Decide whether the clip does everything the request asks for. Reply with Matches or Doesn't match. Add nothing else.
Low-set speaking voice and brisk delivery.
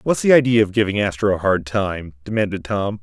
Matches